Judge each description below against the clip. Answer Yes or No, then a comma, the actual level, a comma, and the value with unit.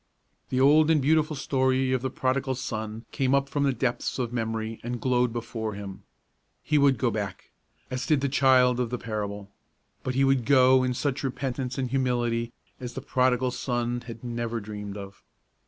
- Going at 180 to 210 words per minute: Yes, average, 185 wpm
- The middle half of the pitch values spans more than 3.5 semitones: No, narrow, 2.5 semitones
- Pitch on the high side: No, low, 125 Hz